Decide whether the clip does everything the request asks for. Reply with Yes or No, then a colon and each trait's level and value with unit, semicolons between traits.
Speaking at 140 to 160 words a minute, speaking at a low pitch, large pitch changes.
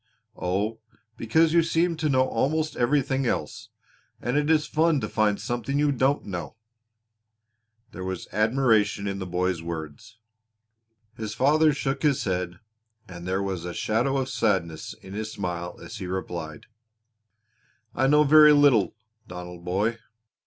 Yes: average, 145 wpm; low, 110 Hz; wide, 7.3 semitones